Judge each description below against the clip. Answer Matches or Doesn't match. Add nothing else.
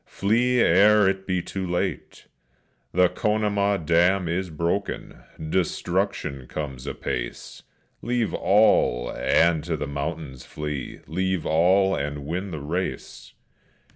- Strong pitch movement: Doesn't match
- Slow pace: Matches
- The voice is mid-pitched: Doesn't match